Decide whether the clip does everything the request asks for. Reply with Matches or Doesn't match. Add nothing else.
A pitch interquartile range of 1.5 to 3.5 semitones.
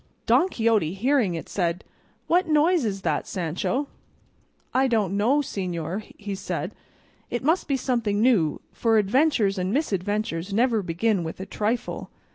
Doesn't match